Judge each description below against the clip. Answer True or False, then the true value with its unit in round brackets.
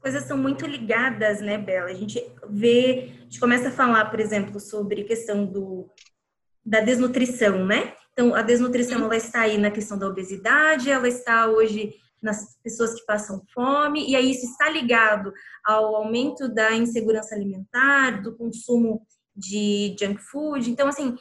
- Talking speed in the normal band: True (160 wpm)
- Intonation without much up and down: False (3.1 semitones)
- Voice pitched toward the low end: False (225 Hz)